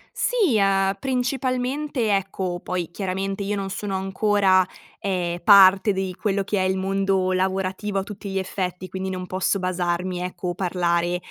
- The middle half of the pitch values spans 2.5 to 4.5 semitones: No, narrow, 1.6 semitones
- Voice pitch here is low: No, high, 190 Hz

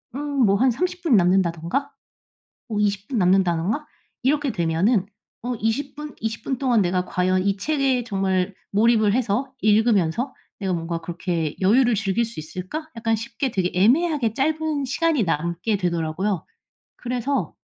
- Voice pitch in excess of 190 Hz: Yes, high, 215 Hz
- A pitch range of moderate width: No, wide, 6.2 semitones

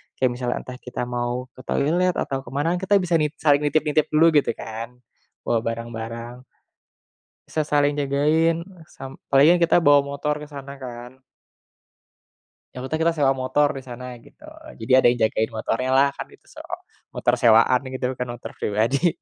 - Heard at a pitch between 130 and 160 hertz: Yes, low, 135 Hz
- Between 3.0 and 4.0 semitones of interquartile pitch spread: Yes, average, 3.4 semitones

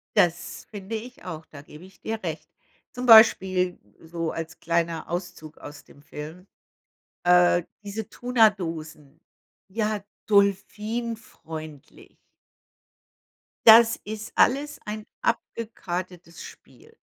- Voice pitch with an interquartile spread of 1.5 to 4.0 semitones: No, average, 5.0 semitones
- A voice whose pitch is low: No, medium, 185 Hz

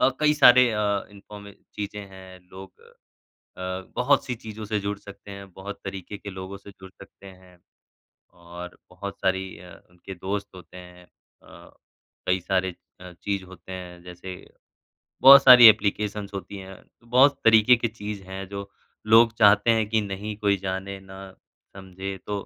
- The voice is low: Yes, low, 100 Hz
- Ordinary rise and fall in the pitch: No, narrow, 2.1 semitones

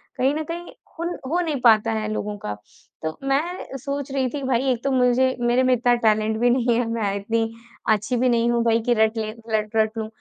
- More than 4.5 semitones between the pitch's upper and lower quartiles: No, average, 3.0 semitones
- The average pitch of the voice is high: Yes, high, 240 Hz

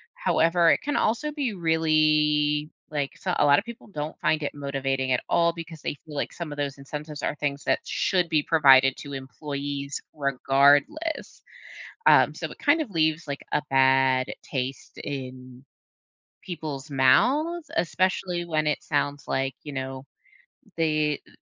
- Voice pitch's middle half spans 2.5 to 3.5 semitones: Yes, average, 3.2 semitones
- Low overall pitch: No, medium, 150 Hz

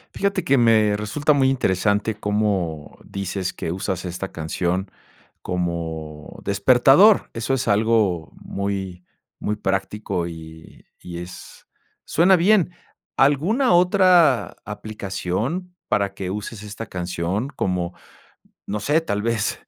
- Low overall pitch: Yes, low, 105 Hz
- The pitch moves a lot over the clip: Yes, wide, 6.7 semitones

